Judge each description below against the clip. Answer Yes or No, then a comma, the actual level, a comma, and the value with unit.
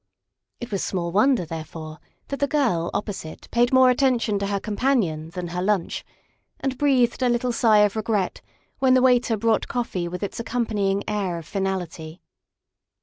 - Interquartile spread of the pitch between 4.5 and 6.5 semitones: Yes, wide, 5.4 semitones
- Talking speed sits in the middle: Yes, average, 175 wpm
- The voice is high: Yes, high, 210 Hz